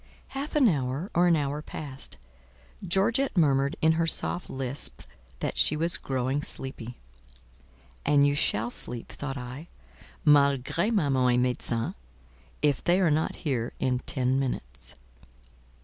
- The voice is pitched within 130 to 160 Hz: Yes, medium, 140 Hz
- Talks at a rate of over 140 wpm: No, slow, 135 wpm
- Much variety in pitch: No, average, 4.3 semitones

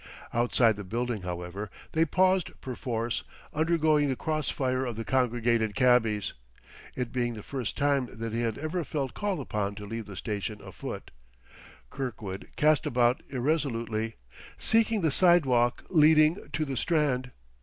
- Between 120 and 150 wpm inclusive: Yes, average, 145 wpm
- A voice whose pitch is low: Yes, low, 125 Hz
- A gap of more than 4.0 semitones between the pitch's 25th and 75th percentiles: Yes, average, 5.2 semitones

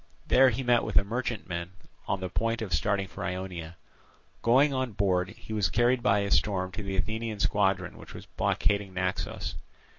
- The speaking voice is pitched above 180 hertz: No, low, 100 Hz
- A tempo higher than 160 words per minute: Yes, average, 180 wpm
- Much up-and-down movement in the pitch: No, average, 3.7 semitones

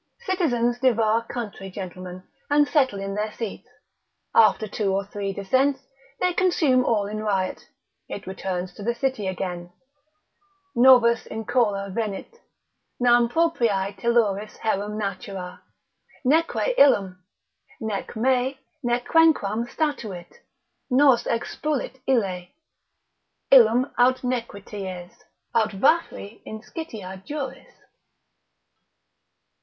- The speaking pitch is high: Yes, high, 225 Hz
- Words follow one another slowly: Yes, slow, 100 wpm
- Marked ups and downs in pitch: No, average, 4.7 semitones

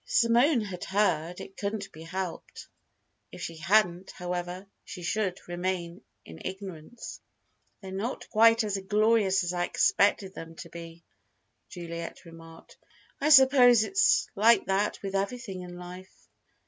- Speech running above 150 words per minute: No, average, 140 wpm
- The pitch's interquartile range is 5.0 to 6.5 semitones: No, average, 3.5 semitones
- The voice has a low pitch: No, high, 190 Hz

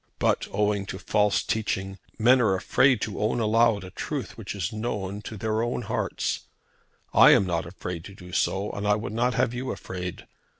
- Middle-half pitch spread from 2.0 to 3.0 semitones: Yes, average, 2.7 semitones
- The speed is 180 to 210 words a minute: Yes, average, 195 wpm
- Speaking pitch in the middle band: No, low, 105 Hz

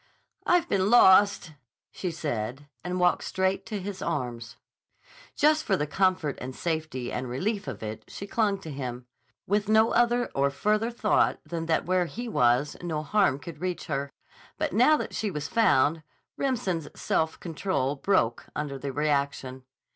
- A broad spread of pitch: Yes, wide, 6.5 semitones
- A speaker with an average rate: Yes, average, 160 wpm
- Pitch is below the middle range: No, medium, 170 Hz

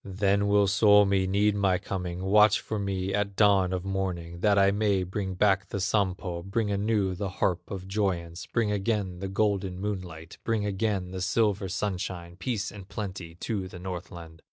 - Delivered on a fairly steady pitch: Yes, narrow, 1.9 semitones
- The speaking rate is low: No, average, 175 wpm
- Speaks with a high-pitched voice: No, very low, 95 Hz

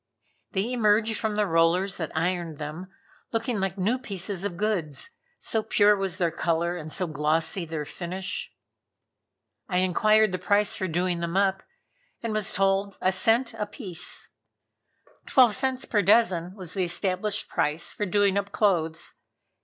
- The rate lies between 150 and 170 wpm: Yes, average, 155 wpm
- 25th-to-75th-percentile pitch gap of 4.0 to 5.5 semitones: No, average, 3.5 semitones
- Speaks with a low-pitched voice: No, high, 190 Hz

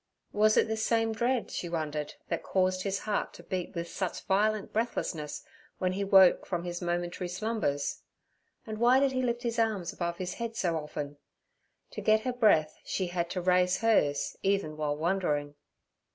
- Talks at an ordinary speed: Yes, average, 180 wpm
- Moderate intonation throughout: Yes, average, 4.3 semitones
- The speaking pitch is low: No, medium, 185 Hz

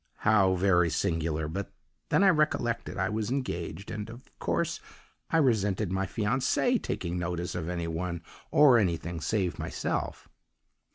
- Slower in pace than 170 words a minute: Yes, average, 145 wpm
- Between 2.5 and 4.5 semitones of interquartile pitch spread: No, average, 5.2 semitones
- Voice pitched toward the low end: Yes, very low, 95 Hz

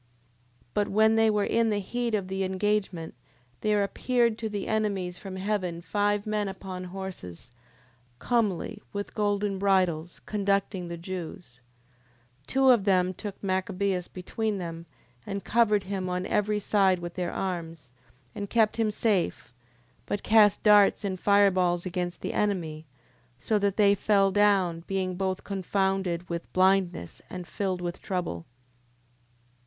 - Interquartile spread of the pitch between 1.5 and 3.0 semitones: Yes, narrow, 2.5 semitones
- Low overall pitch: No, high, 195 Hz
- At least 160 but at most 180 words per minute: No, average, 145 wpm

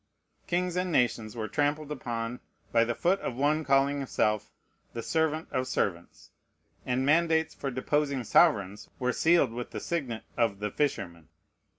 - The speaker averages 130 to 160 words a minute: Yes, average, 155 wpm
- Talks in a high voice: No, low, 130 Hz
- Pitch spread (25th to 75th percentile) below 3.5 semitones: No, average, 5.0 semitones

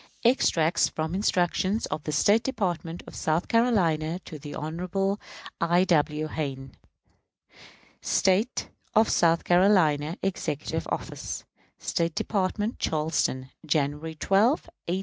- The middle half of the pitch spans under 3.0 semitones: No, average, 4.0 semitones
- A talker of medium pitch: Yes, medium, 170 Hz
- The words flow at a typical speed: No, slow, 110 wpm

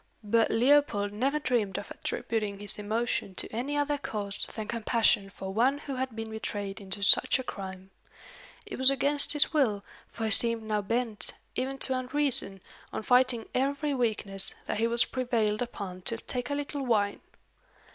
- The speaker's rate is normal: Yes, average, 170 wpm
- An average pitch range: Yes, average, 4.2 semitones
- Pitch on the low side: No, high, 230 Hz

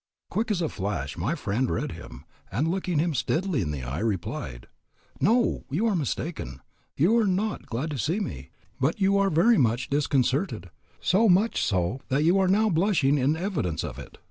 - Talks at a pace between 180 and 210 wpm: Yes, average, 190 wpm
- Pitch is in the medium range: Yes, medium, 155 Hz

